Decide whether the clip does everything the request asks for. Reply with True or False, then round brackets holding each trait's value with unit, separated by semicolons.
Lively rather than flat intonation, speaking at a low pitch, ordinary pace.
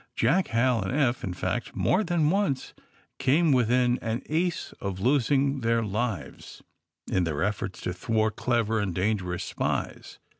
True (5.7 semitones; 115 Hz; 150 wpm)